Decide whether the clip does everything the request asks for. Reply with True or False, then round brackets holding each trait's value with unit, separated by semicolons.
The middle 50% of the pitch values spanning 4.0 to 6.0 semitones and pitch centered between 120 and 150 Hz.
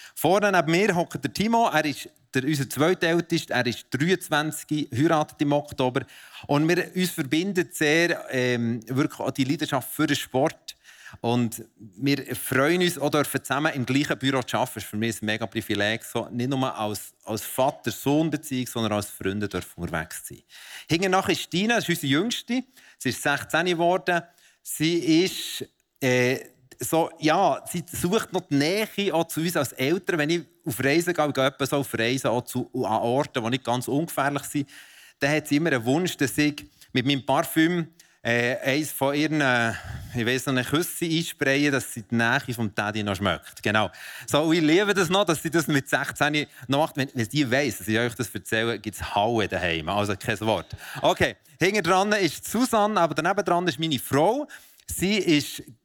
True (5.4 semitones; 140 Hz)